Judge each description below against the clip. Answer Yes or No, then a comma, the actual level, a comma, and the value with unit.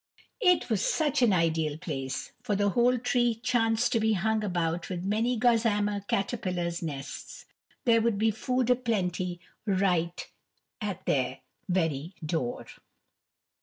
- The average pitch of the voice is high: Yes, high, 205 Hz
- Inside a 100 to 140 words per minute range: Yes, slow, 135 wpm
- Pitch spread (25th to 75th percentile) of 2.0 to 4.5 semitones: No, average, 5.1 semitones